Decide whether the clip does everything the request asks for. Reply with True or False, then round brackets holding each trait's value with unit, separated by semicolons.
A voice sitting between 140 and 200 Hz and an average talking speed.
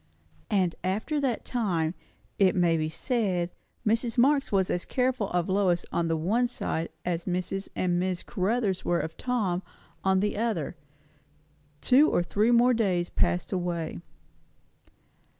True (190 Hz; 145 wpm)